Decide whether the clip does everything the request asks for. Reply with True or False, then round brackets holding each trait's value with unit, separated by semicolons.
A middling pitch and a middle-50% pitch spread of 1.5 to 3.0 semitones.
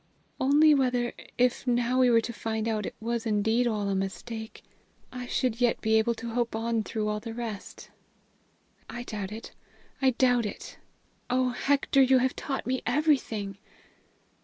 False (235 Hz; 2.4 semitones)